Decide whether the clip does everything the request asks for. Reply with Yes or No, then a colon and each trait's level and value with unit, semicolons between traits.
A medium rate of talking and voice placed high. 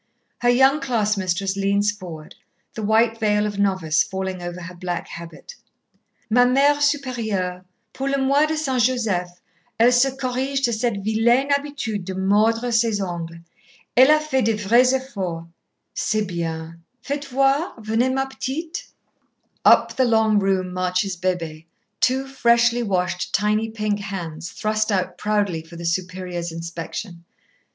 Yes: average, 145 wpm; high, 210 Hz